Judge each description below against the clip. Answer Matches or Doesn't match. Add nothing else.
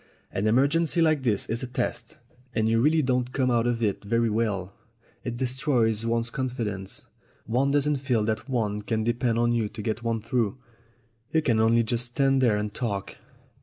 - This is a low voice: Matches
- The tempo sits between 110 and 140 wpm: Doesn't match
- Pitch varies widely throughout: Doesn't match